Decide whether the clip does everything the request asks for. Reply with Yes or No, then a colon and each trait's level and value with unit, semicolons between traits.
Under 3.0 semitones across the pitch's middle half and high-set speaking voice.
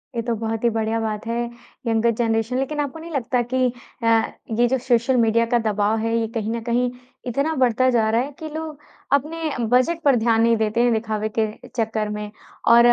Yes: narrow, 2.5 semitones; high, 235 Hz